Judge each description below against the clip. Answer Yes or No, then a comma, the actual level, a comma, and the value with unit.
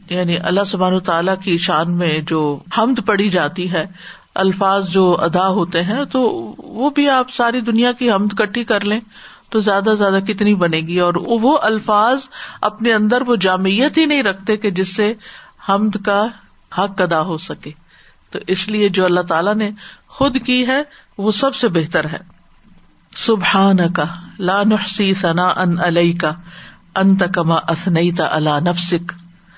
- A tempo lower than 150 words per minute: No, average, 165 wpm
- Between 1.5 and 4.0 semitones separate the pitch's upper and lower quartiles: Yes, average, 3.7 semitones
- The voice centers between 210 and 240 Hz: No, high, 195 Hz